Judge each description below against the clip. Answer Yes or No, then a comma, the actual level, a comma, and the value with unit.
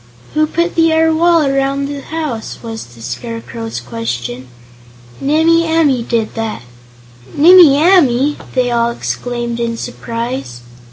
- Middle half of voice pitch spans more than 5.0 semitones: Yes, wide, 5.5 semitones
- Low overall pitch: No, very high, 255 Hz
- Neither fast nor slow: No, slow, 125 wpm